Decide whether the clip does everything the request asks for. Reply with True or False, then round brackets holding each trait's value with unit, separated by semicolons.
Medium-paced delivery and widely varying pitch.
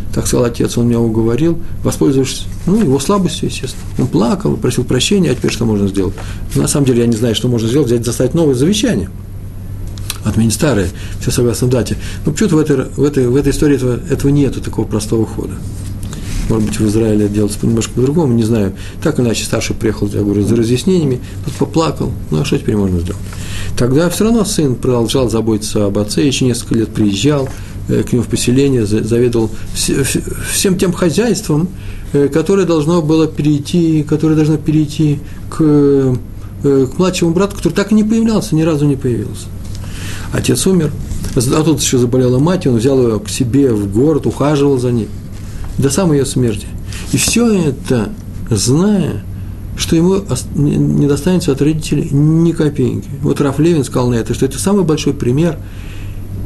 False (175 wpm; 6.8 semitones)